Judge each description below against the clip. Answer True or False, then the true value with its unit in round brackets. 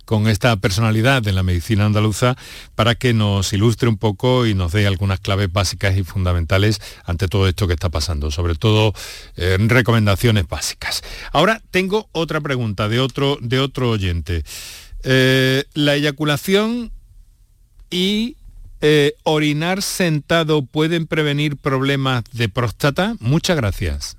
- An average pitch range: False (6.9 semitones)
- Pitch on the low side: True (115 Hz)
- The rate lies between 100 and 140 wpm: True (135 wpm)